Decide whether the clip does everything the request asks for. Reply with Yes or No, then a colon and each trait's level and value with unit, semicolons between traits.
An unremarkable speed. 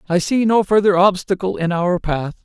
Yes: average, 195 wpm